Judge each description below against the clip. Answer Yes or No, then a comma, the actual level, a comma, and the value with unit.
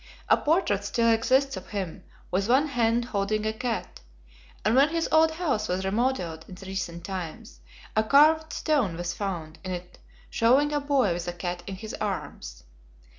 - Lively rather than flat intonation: Yes, wide, 6.4 semitones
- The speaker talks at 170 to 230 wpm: Yes, average, 175 wpm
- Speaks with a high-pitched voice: Yes, high, 215 Hz